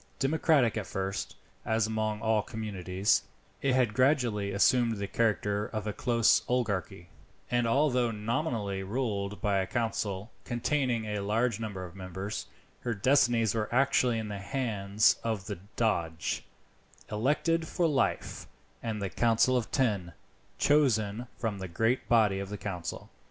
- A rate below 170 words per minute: Yes, average, 145 wpm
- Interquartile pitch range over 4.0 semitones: No, average, 3.4 semitones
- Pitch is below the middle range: Yes, low, 110 Hz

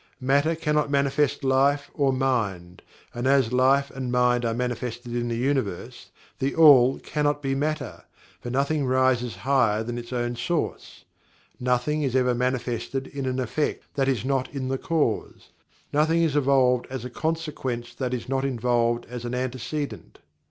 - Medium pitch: No, low, 130 Hz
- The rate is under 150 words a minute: No, average, 160 wpm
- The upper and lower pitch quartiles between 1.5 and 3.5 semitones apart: Yes, narrow, 2.5 semitones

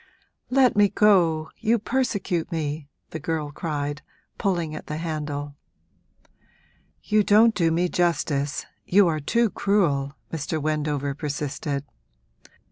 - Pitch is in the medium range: Yes, medium, 160 Hz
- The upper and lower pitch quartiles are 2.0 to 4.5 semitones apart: No, average, 5.1 semitones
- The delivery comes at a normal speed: No, slow, 120 wpm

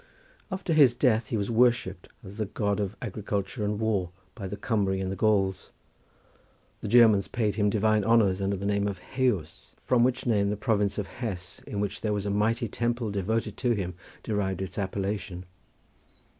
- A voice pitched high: No, low, 105 Hz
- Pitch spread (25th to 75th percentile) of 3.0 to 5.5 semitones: No, narrow, 2.6 semitones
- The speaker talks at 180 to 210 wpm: Yes, average, 185 wpm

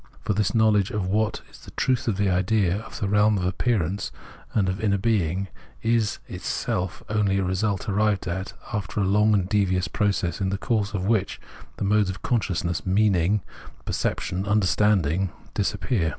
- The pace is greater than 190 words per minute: Yes, average, 200 wpm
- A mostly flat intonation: Yes, narrow, 2.3 semitones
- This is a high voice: No, low, 100 Hz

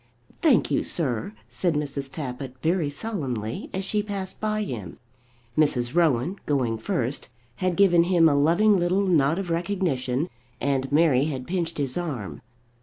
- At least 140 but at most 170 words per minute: Yes, average, 150 wpm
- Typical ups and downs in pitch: No, wide, 5.7 semitones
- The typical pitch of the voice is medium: Yes, medium, 155 Hz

